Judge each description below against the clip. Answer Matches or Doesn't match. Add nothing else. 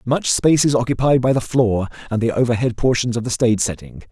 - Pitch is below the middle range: Matches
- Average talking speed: Doesn't match